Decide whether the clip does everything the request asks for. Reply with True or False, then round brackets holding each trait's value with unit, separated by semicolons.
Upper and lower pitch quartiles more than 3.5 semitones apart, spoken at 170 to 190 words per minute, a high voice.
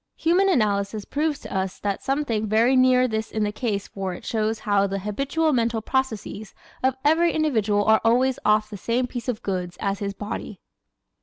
True (4.1 semitones; 185 wpm; 220 Hz)